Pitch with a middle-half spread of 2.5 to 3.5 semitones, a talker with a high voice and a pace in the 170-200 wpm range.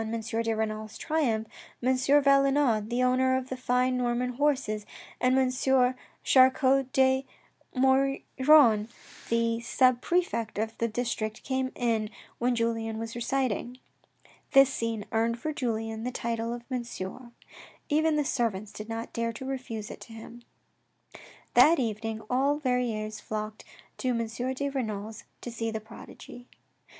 No: average, 2.8 semitones; high, 240 Hz; average, 140 wpm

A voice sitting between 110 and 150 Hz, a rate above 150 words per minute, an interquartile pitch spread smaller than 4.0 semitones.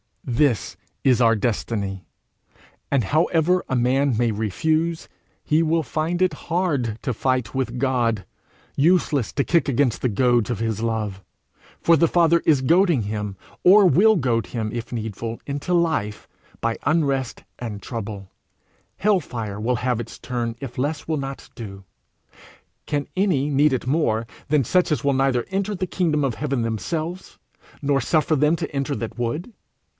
No: low, 135 Hz; average, 160 wpm; wide, 5.6 semitones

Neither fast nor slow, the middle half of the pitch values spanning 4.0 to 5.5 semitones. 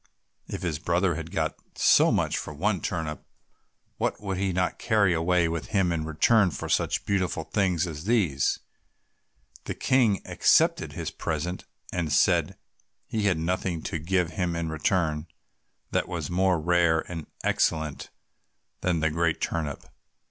No: average, 150 wpm; average, 2.8 semitones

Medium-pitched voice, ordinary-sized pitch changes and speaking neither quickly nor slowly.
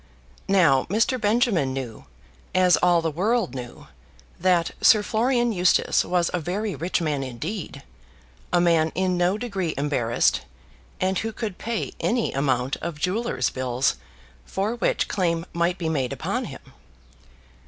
No: medium, 175 Hz; wide, 5.9 semitones; average, 145 wpm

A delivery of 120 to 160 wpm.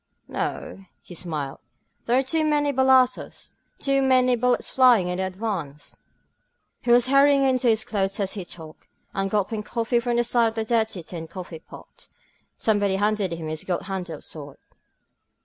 No: average, 175 wpm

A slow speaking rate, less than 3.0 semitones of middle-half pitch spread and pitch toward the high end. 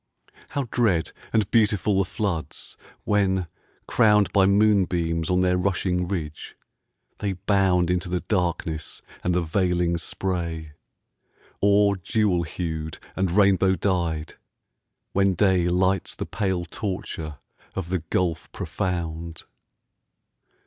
No: slow, 115 wpm; narrow, 2.6 semitones; very low, 90 Hz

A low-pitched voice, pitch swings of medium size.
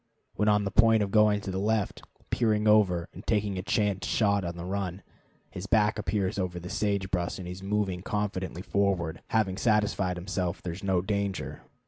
No: low, 100 Hz; narrow, 2.3 semitones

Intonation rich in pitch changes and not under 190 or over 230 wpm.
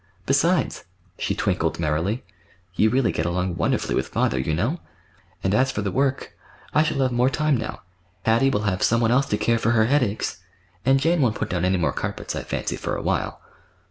Yes: wide, 6.2 semitones; average, 195 wpm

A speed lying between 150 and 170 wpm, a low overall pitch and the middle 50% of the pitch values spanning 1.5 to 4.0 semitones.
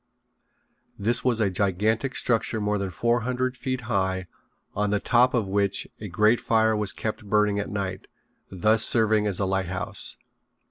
Yes: average, 165 wpm; low, 105 Hz; narrow, 2.6 semitones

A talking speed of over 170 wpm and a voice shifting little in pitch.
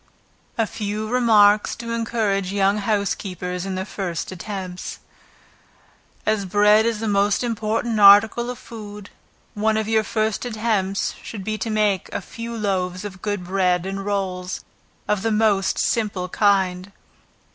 No: average, 145 wpm; narrow, 2.3 semitones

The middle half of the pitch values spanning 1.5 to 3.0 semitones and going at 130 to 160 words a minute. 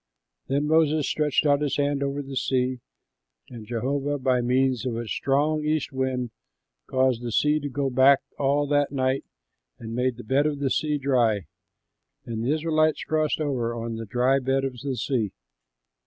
No: narrow, 2.6 semitones; average, 175 wpm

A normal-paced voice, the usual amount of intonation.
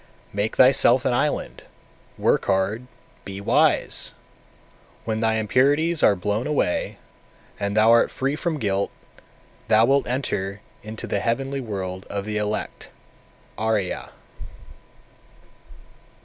No: slow, 120 wpm; average, 4.3 semitones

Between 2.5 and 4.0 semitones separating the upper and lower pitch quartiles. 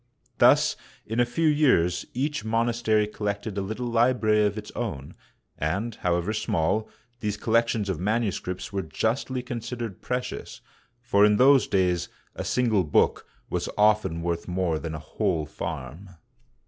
No: average, 4.7 semitones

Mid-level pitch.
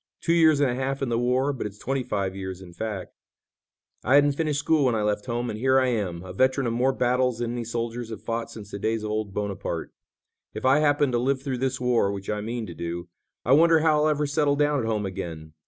No: low, 120 Hz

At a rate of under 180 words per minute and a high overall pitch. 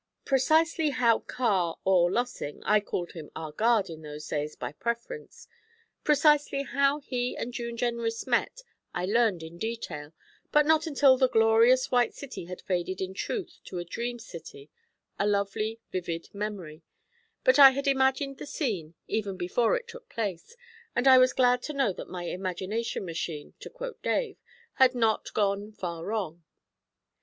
Yes: average, 165 wpm; high, 225 Hz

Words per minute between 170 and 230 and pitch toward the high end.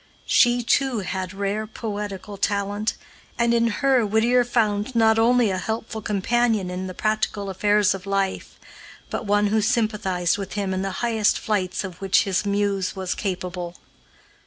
No: average, 160 wpm; high, 205 Hz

